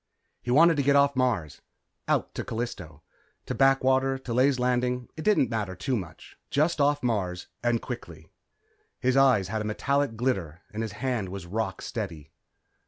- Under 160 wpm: No, average, 170 wpm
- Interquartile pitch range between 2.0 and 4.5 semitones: No, average, 5.3 semitones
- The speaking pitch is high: No, low, 120 Hz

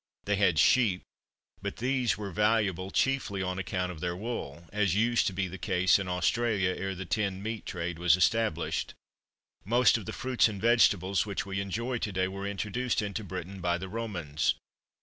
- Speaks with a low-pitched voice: Yes, low, 100 Hz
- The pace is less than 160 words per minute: No, average, 185 wpm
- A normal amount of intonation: Yes, average, 3.5 semitones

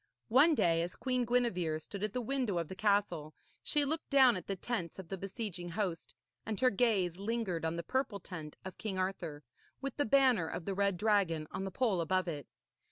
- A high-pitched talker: Yes, high, 195 Hz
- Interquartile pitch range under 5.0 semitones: No, wide, 5.5 semitones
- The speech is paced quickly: Yes, fast, 210 wpm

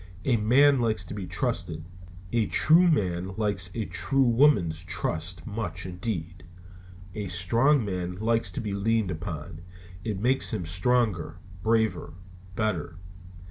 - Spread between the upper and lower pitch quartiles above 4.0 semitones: Yes, average, 4.4 semitones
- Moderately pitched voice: No, low, 100 Hz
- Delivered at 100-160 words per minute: Yes, slow, 135 wpm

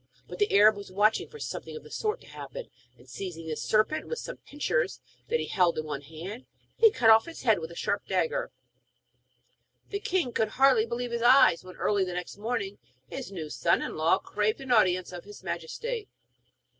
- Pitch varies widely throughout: Yes, wide, 7.1 semitones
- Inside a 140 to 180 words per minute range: No, fast, 205 wpm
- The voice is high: Yes, high, 215 Hz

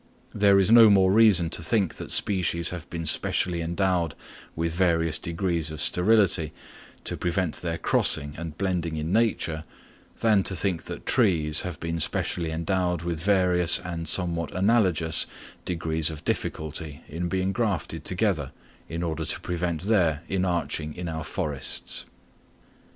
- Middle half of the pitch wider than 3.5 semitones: No, average, 2.7 semitones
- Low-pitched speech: Yes, very low, 85 Hz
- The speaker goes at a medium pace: Yes, average, 145 wpm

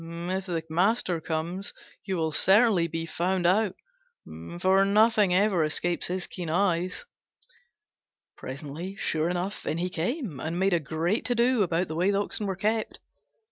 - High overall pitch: No, medium, 180 Hz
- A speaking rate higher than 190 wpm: No, average, 160 wpm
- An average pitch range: Yes, average, 3.2 semitones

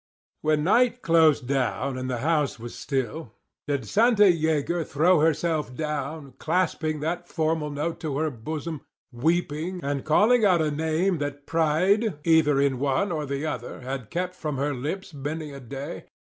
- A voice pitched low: No, medium, 155 Hz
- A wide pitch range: No, average, 3.2 semitones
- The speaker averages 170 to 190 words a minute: No, average, 160 wpm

